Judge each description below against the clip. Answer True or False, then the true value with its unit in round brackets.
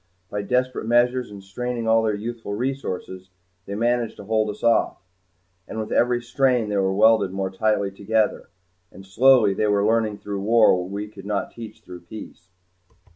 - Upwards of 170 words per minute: True (180 wpm)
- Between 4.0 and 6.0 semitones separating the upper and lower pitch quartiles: False (3.0 semitones)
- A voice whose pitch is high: False (110 Hz)